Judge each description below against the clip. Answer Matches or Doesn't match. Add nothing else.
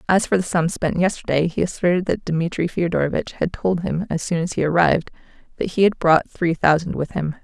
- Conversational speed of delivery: Doesn't match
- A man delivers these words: Doesn't match